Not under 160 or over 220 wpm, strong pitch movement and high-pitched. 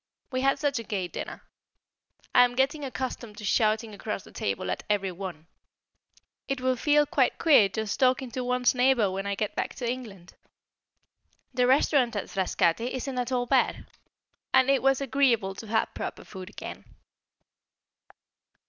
No: average, 165 wpm; average, 4.3 semitones; high, 245 Hz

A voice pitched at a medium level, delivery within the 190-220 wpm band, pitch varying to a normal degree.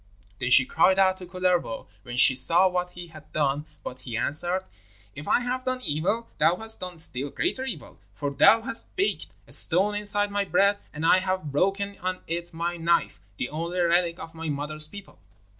Yes: medium, 175 Hz; average, 195 wpm; average, 4.4 semitones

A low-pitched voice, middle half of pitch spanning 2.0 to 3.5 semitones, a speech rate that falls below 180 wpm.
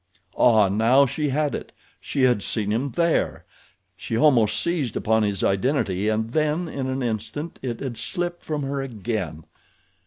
No: low, 125 Hz; average, 5.1 semitones; average, 160 wpm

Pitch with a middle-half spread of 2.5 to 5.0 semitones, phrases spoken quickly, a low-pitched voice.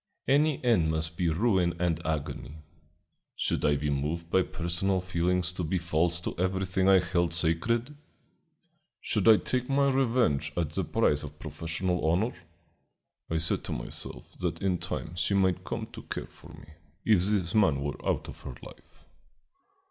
No: average, 3.4 semitones; average, 165 wpm; very low, 90 Hz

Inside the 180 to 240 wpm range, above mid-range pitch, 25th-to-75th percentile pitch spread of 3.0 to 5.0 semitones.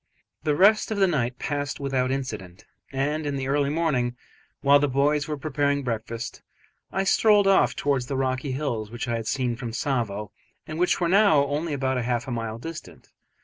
No: average, 190 wpm; medium, 140 Hz; average, 3.7 semitones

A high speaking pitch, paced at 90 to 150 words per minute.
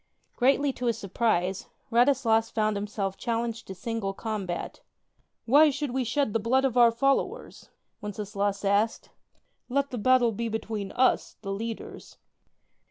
Yes: high, 225 Hz; average, 145 wpm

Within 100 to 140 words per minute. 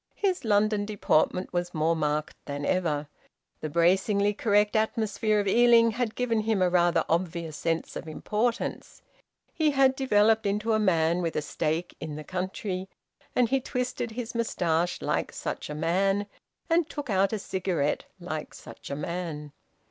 No: average, 160 wpm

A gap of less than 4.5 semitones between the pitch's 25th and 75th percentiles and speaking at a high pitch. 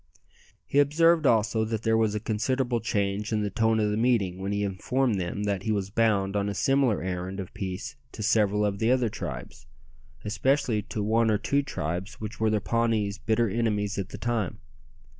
No: narrow, 2.5 semitones; low, 110 Hz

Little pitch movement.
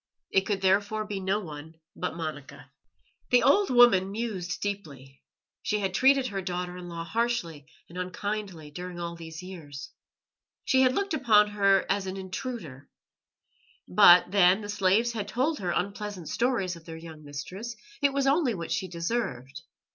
No: average, 4.3 semitones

